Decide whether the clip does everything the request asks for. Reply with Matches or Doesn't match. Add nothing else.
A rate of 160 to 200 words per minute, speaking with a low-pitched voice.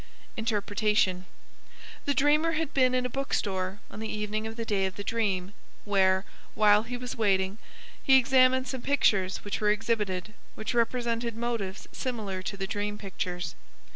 Doesn't match